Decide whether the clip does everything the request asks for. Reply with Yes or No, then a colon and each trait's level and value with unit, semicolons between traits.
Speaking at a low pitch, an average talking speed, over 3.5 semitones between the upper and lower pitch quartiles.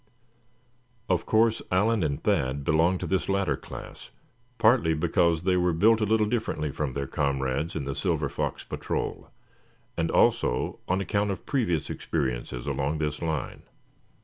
Yes: very low, 80 Hz; average, 150 wpm; wide, 5.6 semitones